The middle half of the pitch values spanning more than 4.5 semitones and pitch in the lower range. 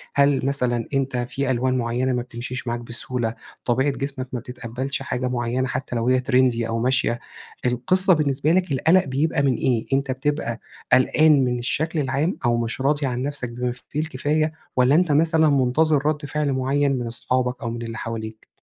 No: average, 2.8 semitones; low, 130 Hz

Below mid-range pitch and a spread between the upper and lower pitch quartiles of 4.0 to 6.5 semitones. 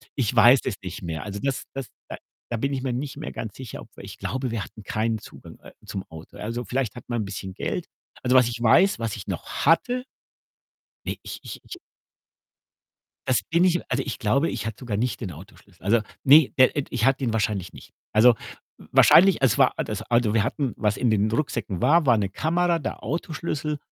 Yes: low, 120 Hz; average, 4.7 semitones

